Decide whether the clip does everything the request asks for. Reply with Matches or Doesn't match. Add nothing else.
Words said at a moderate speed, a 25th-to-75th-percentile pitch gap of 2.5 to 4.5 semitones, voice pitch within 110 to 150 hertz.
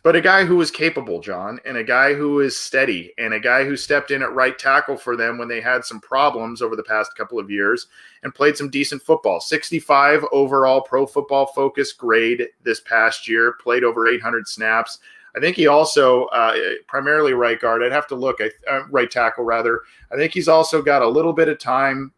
Doesn't match